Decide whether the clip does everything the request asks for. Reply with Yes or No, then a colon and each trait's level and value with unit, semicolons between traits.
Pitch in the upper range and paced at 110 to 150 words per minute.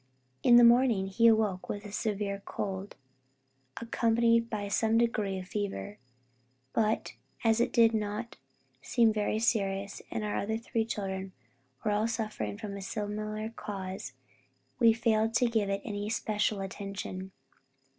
Yes: high, 215 Hz; average, 140 wpm